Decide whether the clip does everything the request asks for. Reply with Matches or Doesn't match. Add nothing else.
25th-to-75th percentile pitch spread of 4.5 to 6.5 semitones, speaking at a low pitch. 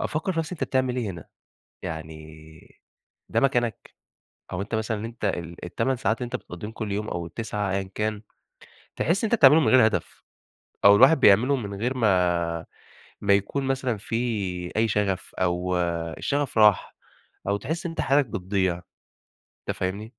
Matches